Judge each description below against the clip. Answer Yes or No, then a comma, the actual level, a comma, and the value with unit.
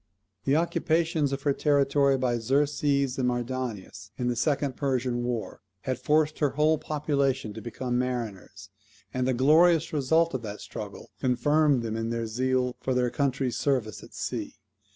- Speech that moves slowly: No, average, 160 wpm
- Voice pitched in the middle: No, low, 130 Hz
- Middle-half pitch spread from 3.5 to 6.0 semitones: No, average, 3.1 semitones